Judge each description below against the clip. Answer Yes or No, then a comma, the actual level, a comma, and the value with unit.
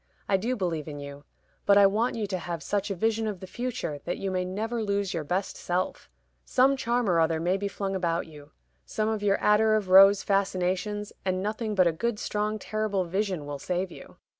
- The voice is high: Yes, high, 195 Hz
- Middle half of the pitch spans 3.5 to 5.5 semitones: No, average, 3.1 semitones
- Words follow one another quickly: Yes, fast, 215 wpm